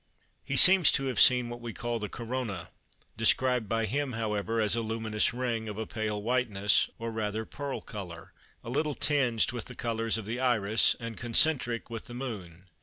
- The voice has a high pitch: No, low, 115 Hz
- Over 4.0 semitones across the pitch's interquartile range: No, narrow, 2.5 semitones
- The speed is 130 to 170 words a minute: No, average, 185 wpm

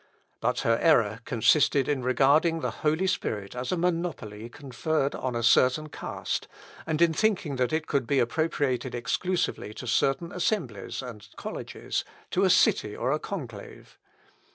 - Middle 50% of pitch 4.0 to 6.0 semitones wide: Yes, average, 5.1 semitones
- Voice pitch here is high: No, low, 135 Hz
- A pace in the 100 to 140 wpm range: No, average, 155 wpm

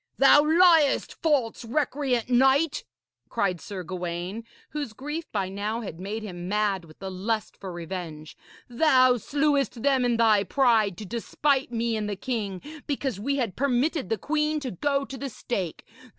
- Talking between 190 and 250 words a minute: No, average, 165 wpm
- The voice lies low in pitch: No, high, 230 Hz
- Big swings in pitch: Yes, wide, 6.0 semitones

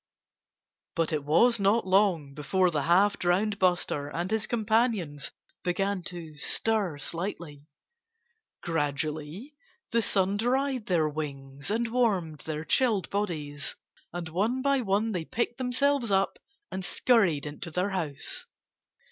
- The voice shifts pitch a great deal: Yes, wide, 6.0 semitones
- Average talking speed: No, slow, 130 wpm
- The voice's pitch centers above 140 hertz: Yes, medium, 185 Hz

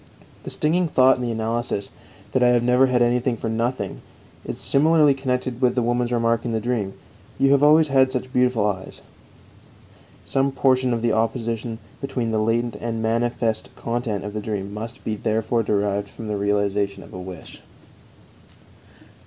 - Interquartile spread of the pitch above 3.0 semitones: No, average, 2.7 semitones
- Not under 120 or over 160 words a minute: No, average, 170 wpm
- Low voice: Yes, low, 115 Hz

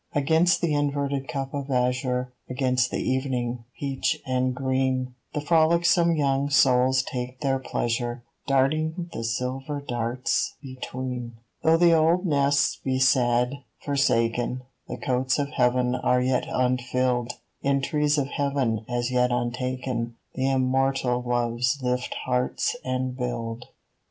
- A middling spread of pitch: No, narrow, 2.1 semitones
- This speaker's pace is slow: Yes, slow, 130 wpm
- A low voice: Yes, low, 130 Hz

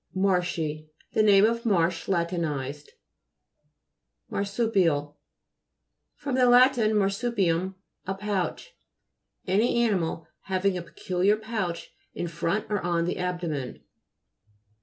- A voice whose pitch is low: No, high, 190 Hz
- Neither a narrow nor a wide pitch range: Yes, average, 4.1 semitones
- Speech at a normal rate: No, slow, 110 wpm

